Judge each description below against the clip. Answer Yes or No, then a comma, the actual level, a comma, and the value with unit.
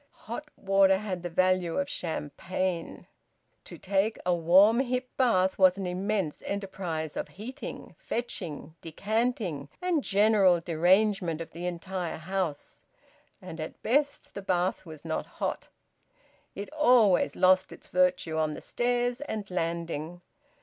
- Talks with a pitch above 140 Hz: Yes, medium, 185 Hz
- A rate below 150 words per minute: Yes, slow, 135 wpm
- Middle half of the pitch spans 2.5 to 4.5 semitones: Yes, average, 4.1 semitones